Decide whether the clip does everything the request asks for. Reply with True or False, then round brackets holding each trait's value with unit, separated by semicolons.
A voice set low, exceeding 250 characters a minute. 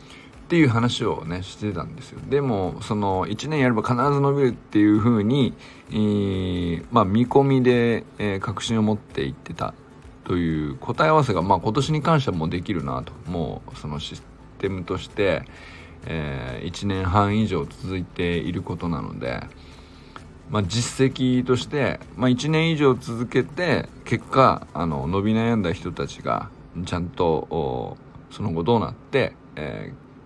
True (110 Hz; 295 characters per minute)